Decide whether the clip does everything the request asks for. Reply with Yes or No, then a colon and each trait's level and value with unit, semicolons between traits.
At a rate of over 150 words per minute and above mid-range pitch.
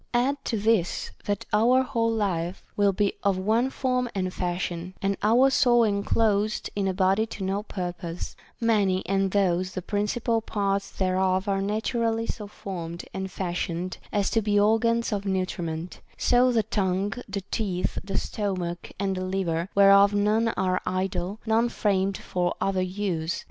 Yes: average, 160 wpm; high, 200 Hz